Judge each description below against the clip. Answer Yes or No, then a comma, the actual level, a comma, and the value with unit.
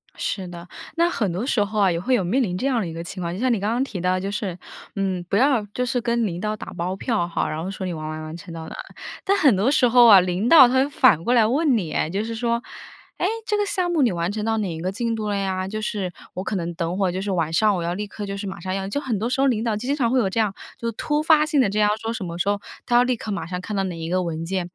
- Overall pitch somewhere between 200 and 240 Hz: Yes, high, 205 Hz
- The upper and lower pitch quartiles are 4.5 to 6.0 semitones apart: Yes, average, 4.9 semitones